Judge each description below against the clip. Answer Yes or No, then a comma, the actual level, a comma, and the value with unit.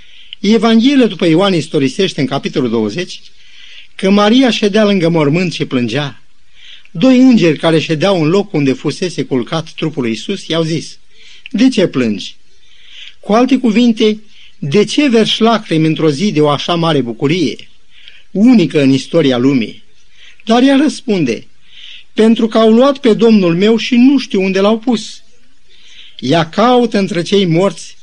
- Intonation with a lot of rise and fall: Yes, wide, 6.3 semitones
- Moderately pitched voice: No, high, 195 Hz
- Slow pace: No, average, 150 wpm